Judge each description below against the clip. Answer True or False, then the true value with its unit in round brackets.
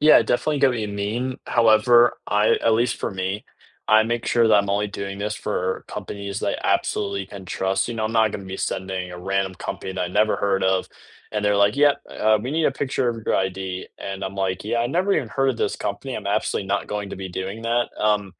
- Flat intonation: False (3.2 semitones)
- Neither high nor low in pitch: False (105 Hz)